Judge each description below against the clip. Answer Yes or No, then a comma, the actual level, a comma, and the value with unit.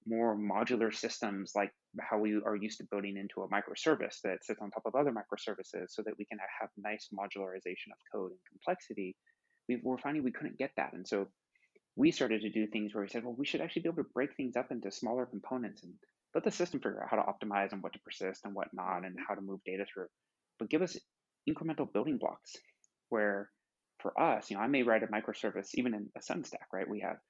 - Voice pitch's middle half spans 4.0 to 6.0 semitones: No, average, 3.2 semitones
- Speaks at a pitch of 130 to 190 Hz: No, low, 105 Hz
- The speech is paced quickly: Yes, fast, 235 wpm